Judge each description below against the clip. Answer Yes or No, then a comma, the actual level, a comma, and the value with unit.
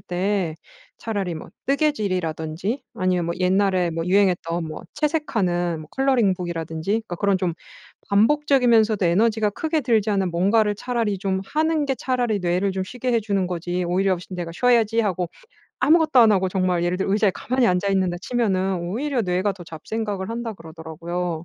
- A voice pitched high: Yes, high, 195 Hz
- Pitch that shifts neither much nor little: Yes, average, 4.4 semitones